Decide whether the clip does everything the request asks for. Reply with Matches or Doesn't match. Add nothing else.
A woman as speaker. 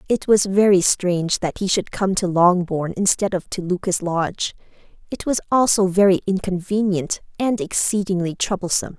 Matches